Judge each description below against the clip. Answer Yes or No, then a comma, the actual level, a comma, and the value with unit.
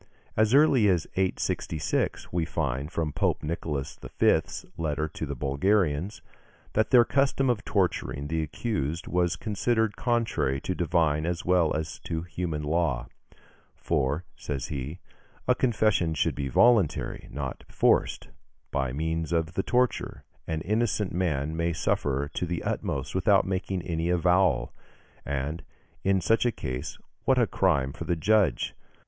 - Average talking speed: Yes, average, 145 wpm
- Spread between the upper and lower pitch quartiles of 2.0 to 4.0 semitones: No, average, 4.7 semitones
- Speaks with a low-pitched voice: Yes, very low, 85 Hz